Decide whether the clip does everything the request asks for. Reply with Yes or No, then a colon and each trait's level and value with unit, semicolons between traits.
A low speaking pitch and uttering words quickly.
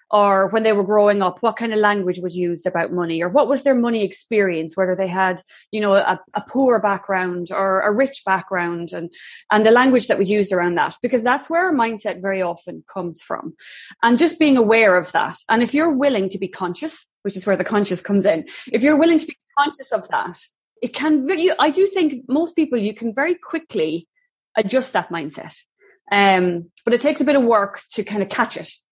No: high, 215 Hz; fast, 210 wpm